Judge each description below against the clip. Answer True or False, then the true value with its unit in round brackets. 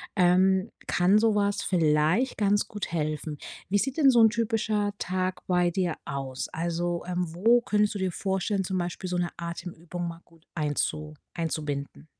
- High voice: False (180 Hz)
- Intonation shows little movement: False (3.5 semitones)